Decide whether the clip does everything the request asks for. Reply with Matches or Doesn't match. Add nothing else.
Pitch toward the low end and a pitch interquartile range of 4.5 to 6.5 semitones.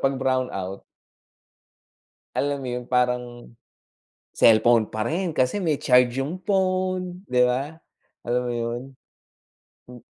Matches